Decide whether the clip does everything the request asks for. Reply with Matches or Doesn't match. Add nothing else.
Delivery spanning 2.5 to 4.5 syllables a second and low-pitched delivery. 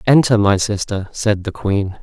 Matches